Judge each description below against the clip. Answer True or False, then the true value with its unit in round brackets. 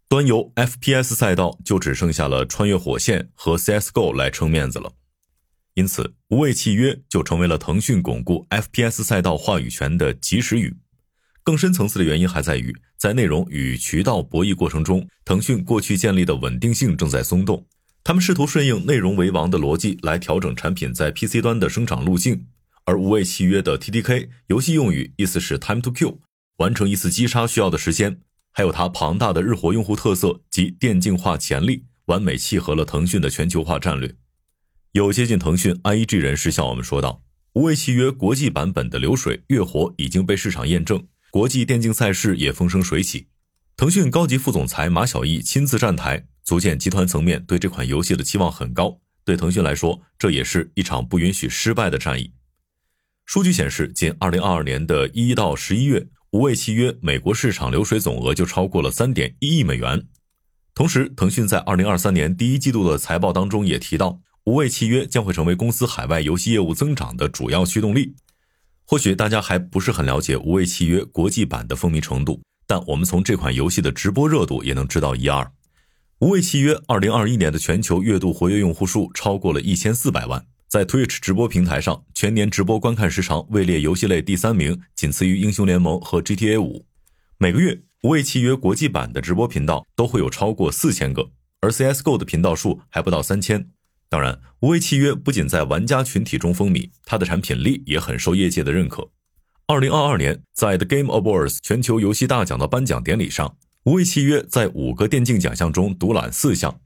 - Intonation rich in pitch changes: True (6.3 semitones)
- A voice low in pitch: True (95 Hz)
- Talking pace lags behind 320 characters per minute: False (325 characters per minute)